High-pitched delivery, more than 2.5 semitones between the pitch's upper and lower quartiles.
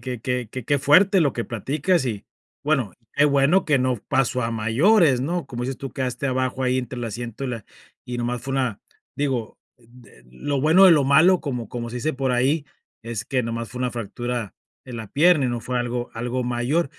No: low, 125 Hz; average, 2.9 semitones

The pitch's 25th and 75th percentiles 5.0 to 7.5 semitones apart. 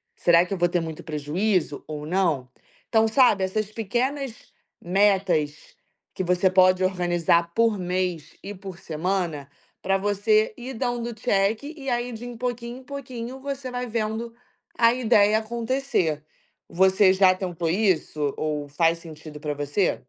Yes: average, 5.3 semitones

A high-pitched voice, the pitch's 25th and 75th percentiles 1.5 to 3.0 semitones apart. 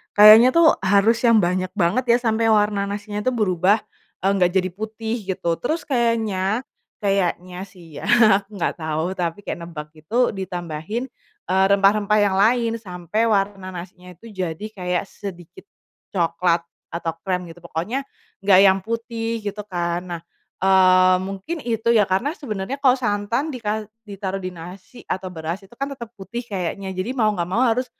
No: high, 195 Hz; average, 3.7 semitones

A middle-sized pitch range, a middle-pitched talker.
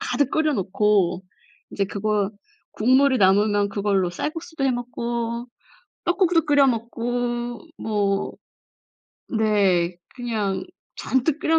No: average, 4.8 semitones; high, 230 Hz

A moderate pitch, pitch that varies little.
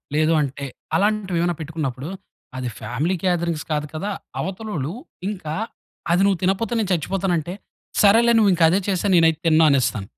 No: medium, 170 Hz; average, 4.2 semitones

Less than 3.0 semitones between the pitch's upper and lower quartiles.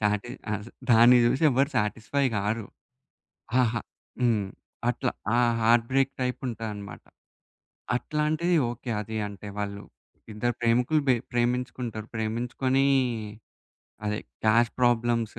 Yes: narrow, 2.6 semitones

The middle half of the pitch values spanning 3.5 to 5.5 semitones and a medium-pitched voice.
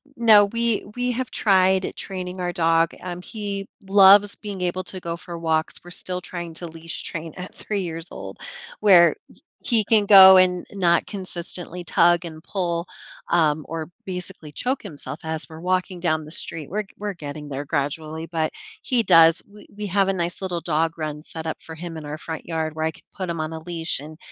No: average, 2.9 semitones; medium, 175 Hz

